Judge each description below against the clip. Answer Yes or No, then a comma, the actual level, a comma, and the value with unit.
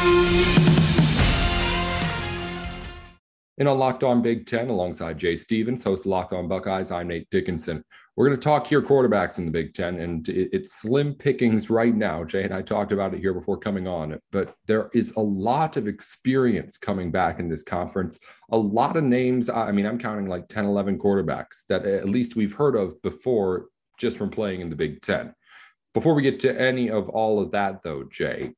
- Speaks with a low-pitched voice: Yes, low, 105 Hz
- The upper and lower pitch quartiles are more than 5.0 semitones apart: Yes, wide, 5.5 semitones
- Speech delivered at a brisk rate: No, average, 190 wpm